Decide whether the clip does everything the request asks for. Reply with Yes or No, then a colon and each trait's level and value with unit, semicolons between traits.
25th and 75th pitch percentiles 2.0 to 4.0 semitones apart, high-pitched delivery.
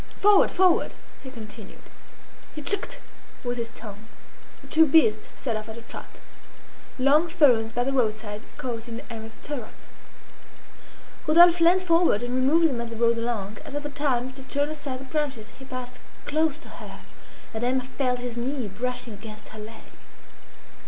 No: average, 4.4 semitones; very high, 250 Hz